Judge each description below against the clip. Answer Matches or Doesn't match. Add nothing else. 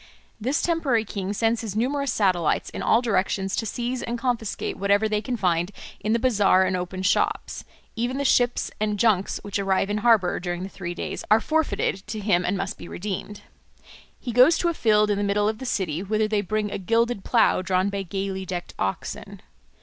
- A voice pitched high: Matches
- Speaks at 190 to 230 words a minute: Matches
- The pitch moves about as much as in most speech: Matches